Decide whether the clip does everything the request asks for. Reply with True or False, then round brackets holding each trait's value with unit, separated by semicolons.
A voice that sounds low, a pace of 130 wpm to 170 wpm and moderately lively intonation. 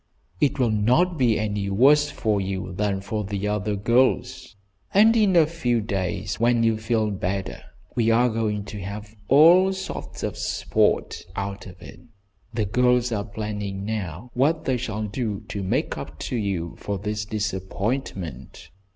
True (110 Hz; 160 wpm; 3.7 semitones)